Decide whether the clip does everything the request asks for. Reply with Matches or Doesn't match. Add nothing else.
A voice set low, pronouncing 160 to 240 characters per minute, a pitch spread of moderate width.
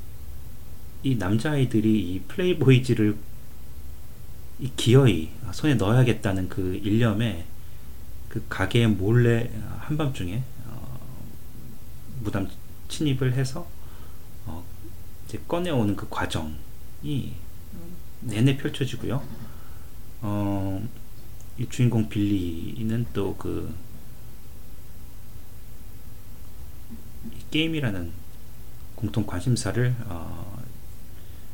Matches